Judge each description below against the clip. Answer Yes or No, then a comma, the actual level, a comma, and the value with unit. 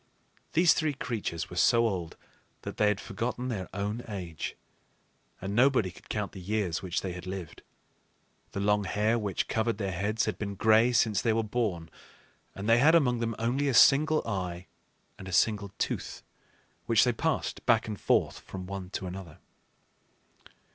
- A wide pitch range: No, average, 3.6 semitones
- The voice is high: No, low, 105 Hz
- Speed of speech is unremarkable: Yes, average, 175 wpm